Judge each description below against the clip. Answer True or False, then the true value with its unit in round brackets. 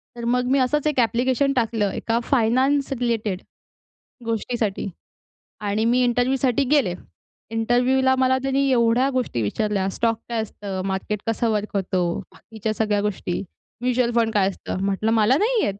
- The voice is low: False (230 Hz)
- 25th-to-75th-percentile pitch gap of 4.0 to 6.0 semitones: False (3.6 semitones)